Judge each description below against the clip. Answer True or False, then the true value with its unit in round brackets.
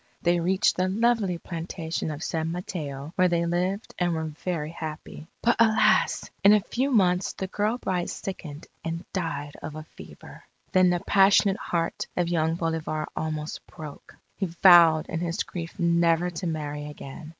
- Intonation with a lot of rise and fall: False (2.8 semitones)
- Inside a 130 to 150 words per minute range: False (165 wpm)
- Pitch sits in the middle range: True (170 Hz)